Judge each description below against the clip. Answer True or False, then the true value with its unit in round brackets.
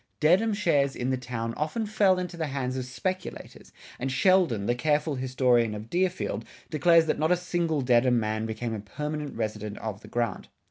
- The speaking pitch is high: False (135 Hz)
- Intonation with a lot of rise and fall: True (6.3 semitones)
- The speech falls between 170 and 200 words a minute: True (185 wpm)